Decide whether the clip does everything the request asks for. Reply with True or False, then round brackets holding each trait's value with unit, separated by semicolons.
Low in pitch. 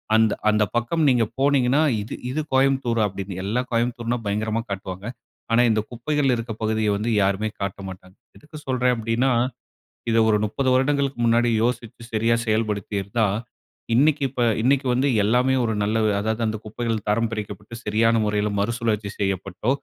True (115 Hz)